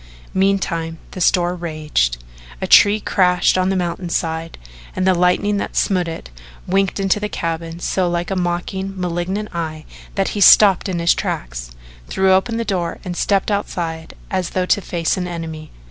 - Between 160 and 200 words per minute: Yes, average, 170 wpm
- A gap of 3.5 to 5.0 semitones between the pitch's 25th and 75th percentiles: No, narrow, 2.5 semitones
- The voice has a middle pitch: Yes, medium, 180 Hz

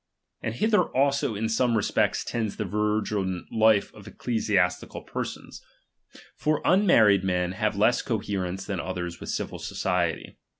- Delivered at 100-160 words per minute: Yes, average, 140 wpm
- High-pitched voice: No, low, 105 Hz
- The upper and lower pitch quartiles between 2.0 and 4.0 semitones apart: Yes, average, 3.4 semitones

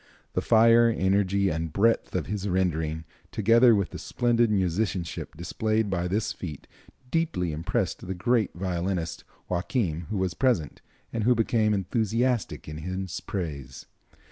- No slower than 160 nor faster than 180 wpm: No, average, 140 wpm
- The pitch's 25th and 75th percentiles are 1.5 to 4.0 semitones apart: No, average, 4.5 semitones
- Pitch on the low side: Yes, very low, 95 Hz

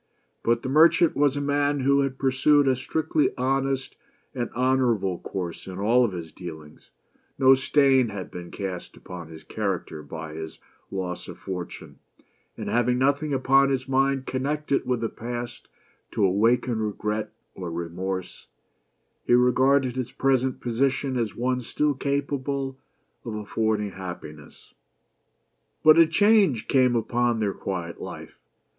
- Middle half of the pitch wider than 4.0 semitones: Yes, wide, 5.6 semitones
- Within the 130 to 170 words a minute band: Yes, average, 140 wpm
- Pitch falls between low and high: No, low, 125 Hz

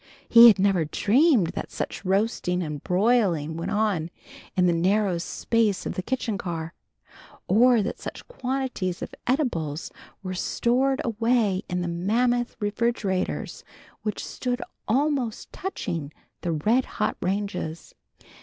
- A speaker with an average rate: No, slow, 130 wpm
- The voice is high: Yes, high, 205 Hz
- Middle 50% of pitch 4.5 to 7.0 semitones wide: Yes, average, 5.2 semitones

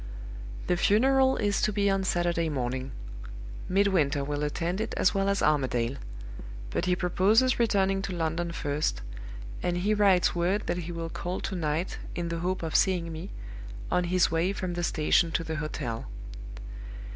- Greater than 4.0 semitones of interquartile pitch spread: No, average, 3.4 semitones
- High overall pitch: No, medium, 175 Hz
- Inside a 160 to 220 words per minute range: Yes, average, 170 wpm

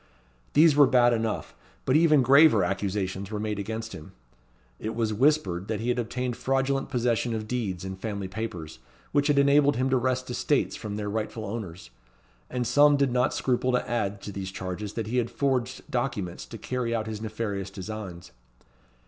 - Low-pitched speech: Yes, low, 115 Hz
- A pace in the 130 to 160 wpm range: No, average, 180 wpm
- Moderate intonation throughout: Yes, average, 4.1 semitones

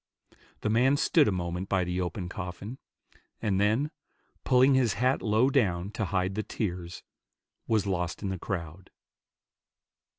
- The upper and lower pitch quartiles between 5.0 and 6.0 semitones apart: No, average, 4.3 semitones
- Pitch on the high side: No, low, 100 Hz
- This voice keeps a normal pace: Yes, average, 145 wpm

